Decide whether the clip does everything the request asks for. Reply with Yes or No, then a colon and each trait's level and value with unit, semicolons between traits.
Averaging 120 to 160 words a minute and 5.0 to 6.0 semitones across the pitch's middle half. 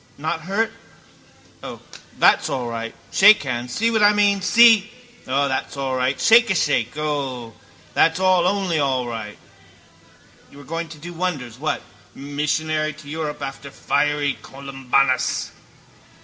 Yes: average, 145 wpm; wide, 5.4 semitones